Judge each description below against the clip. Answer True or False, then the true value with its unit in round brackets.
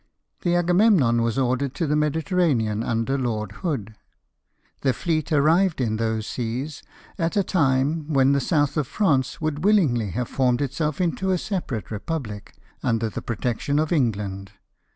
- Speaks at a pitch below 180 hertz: True (140 Hz)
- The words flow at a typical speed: True (155 wpm)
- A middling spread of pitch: False (5.8 semitones)